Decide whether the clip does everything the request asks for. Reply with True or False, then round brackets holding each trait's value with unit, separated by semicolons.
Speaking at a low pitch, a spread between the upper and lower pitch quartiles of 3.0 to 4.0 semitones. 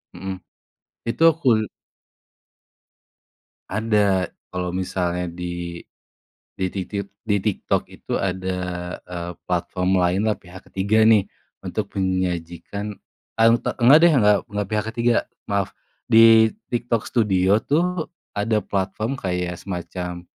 True (100 Hz; 3.4 semitones)